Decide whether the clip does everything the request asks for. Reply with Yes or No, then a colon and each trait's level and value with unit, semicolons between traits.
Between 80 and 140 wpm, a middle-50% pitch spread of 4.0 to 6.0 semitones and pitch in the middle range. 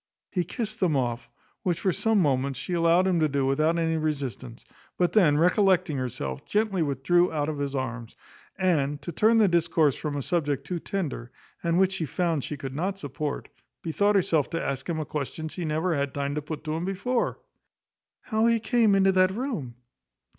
No: average, 195 wpm; average, 4.8 semitones; medium, 160 Hz